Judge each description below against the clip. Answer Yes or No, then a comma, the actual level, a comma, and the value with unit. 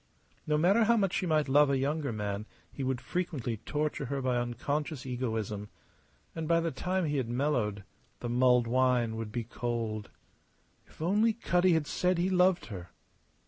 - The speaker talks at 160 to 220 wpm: Yes, average, 175 wpm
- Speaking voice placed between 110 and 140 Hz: Yes, low, 135 Hz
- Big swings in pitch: Yes, wide, 5.9 semitones